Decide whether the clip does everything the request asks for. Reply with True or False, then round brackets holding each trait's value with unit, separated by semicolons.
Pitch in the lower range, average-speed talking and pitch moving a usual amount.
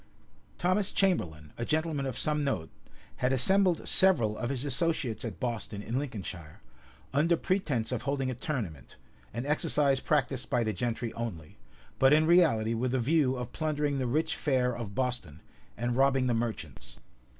True (130 Hz; 160 wpm; 4.5 semitones)